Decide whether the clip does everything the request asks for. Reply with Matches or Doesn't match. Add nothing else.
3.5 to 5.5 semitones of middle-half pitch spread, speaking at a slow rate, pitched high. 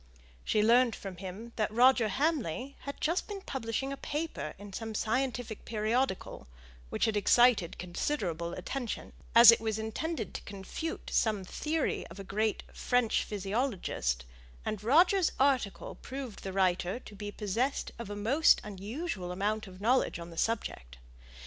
Doesn't match